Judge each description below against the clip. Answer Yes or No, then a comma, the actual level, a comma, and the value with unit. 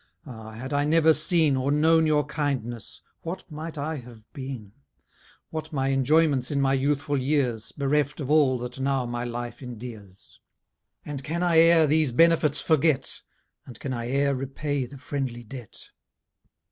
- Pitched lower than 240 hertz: Yes, medium, 140 Hz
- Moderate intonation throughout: Yes, average, 3.5 semitones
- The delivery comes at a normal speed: Yes, average, 160 wpm